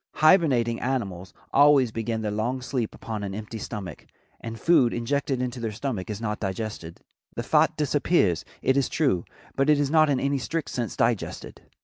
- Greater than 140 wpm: Yes, average, 175 wpm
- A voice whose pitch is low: Yes, low, 120 Hz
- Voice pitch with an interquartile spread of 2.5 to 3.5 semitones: No, average, 4.6 semitones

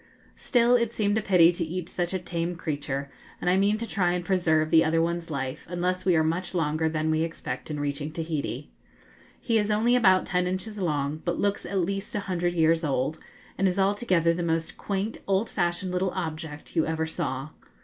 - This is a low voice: No, medium, 175 Hz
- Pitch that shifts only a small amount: No, average, 3.3 semitones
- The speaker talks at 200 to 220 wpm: Yes, fast, 205 wpm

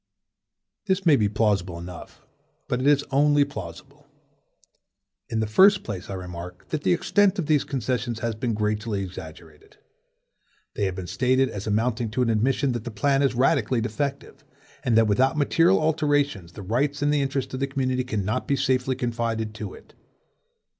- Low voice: Yes, low, 120 Hz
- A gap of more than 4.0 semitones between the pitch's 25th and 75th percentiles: Yes, average, 4.9 semitones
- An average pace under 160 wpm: No, average, 175 wpm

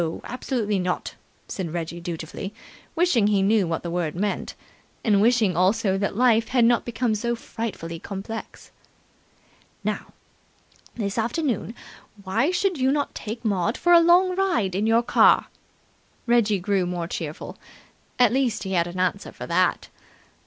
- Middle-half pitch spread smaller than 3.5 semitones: No, average, 4.5 semitones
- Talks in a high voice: Yes, high, 215 Hz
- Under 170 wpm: Yes, average, 150 wpm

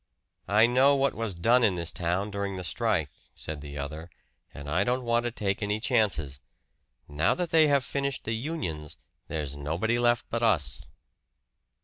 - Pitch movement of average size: No, wide, 7.1 semitones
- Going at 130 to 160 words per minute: No, average, 170 wpm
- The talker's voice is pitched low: Yes, low, 105 Hz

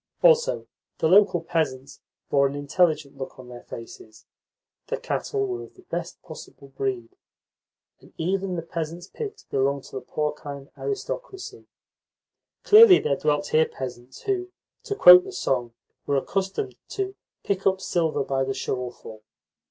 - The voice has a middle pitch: Yes, medium, 155 Hz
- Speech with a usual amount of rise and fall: No, wide, 6.5 semitones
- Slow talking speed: No, average, 145 wpm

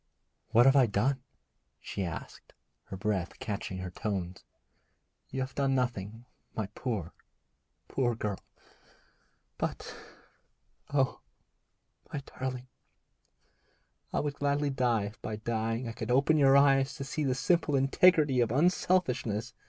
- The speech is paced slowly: Yes, slow, 130 wpm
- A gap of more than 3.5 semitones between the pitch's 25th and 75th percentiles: Yes, average, 4.1 semitones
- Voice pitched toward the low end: Yes, low, 125 Hz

